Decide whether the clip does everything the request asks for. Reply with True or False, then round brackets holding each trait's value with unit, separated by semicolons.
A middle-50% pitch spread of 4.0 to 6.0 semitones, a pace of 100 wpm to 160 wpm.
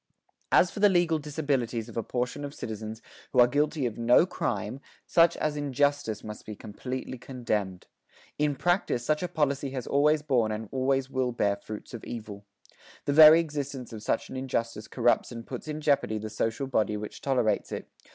False (4.6 semitones; 185 wpm)